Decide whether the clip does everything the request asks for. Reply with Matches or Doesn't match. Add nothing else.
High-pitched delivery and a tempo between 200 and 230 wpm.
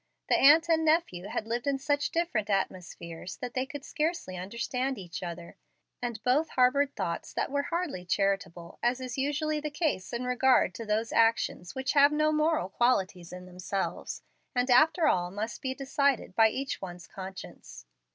Doesn't match